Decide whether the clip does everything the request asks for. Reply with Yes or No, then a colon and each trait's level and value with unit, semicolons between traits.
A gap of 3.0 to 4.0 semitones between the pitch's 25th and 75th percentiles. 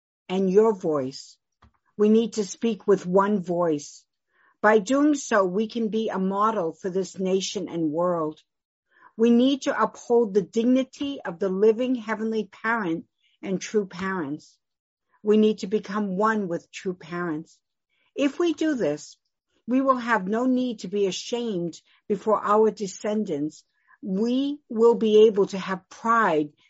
Yes: average, 3.7 semitones